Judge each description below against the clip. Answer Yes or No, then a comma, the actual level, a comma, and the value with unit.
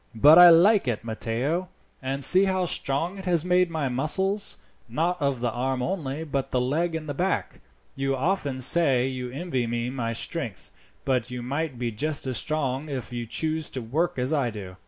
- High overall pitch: No, medium, 140 Hz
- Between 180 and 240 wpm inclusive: Yes, average, 190 wpm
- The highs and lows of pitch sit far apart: No, average, 4.9 semitones